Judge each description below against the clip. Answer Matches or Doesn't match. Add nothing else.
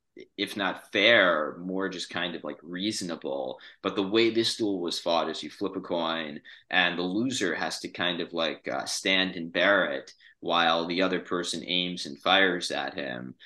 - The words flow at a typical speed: Matches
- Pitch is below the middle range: Matches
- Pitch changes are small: Matches